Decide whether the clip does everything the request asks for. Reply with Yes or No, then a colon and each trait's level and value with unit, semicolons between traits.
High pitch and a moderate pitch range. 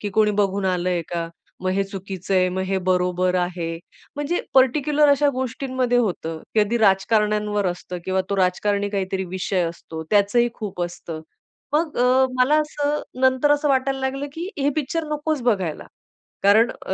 No: high, 210 Hz; wide, 6.2 semitones